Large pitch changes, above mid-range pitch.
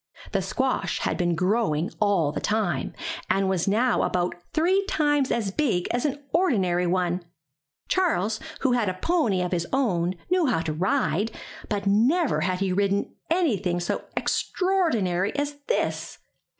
Yes: wide, 7.8 semitones; high, 205 Hz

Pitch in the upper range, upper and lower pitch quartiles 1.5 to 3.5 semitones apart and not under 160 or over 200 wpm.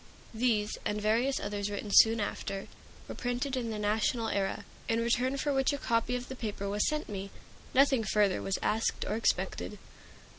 Yes: high, 225 Hz; average, 3.2 semitones; average, 180 wpm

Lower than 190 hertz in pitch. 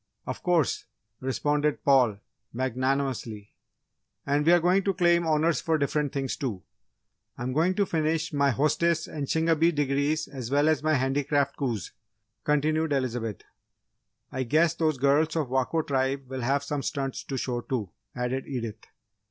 Yes: medium, 140 Hz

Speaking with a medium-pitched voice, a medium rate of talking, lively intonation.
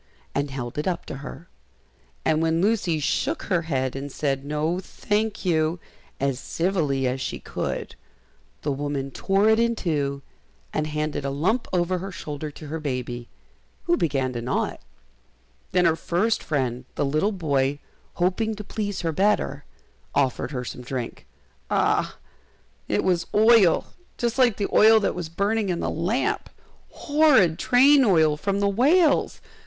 Yes: medium, 165 Hz; average, 160 wpm; wide, 6.4 semitones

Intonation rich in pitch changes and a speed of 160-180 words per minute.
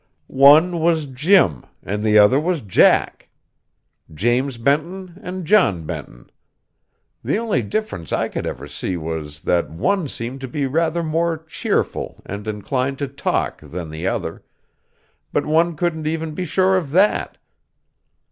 No: wide, 8.4 semitones; average, 145 wpm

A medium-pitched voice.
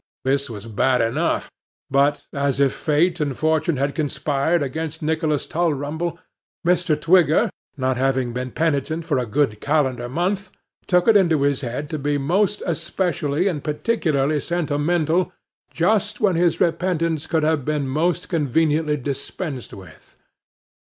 Yes: medium, 150 Hz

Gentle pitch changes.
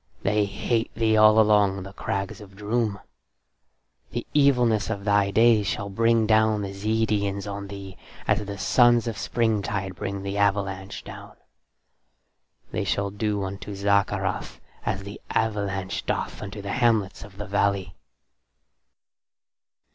Yes: narrow, 1.8 semitones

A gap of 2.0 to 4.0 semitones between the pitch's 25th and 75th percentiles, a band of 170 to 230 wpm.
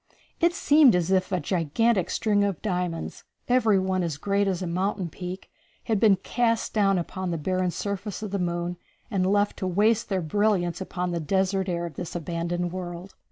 Yes: narrow, 2.6 semitones; average, 190 wpm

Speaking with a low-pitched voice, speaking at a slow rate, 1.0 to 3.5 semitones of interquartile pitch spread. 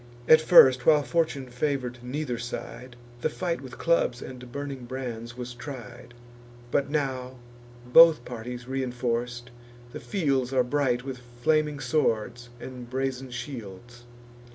Yes: low, 125 Hz; slow, 130 wpm; average, 2.7 semitones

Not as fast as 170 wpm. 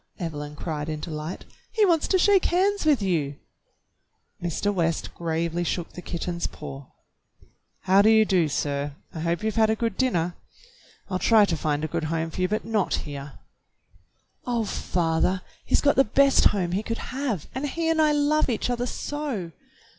No: average, 185 wpm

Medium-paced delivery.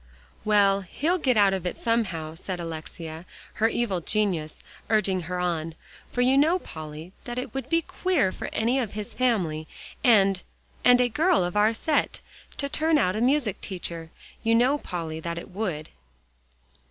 Yes: average, 170 wpm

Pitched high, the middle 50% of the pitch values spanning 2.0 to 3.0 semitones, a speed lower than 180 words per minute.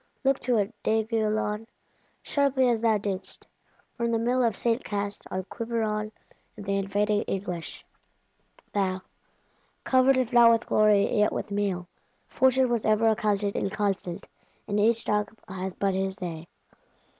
Yes: high, 210 Hz; narrow, 2.6 semitones; average, 145 wpm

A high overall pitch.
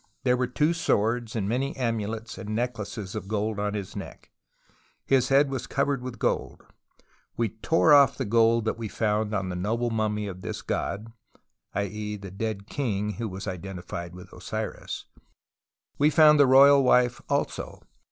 No: low, 110 Hz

